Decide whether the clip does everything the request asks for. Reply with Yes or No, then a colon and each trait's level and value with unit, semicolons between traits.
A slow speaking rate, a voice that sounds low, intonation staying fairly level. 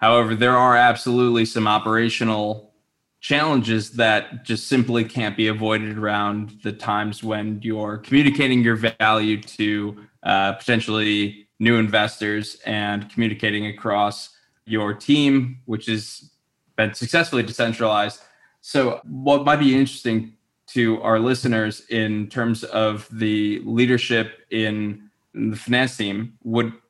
Yes: slow, 120 wpm; low, 110 Hz; narrow, 2.1 semitones